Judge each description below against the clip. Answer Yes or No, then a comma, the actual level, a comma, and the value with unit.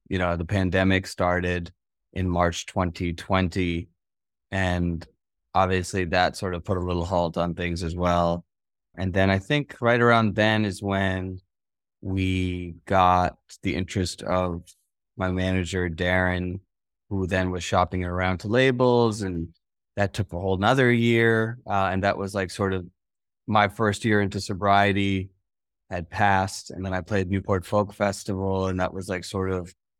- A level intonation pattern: Yes, narrow, 1.9 semitones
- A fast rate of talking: No, average, 160 wpm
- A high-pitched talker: No, very low, 95 Hz